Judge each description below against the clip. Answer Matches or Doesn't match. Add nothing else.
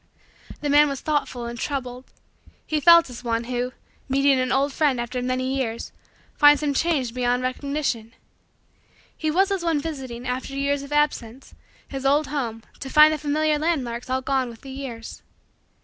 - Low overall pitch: Doesn't match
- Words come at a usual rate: Matches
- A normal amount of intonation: Matches